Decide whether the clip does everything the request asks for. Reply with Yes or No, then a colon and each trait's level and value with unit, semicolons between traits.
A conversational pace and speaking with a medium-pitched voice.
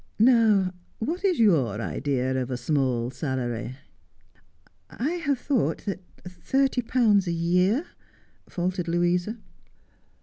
No: slow, 130 wpm; medium, 180 Hz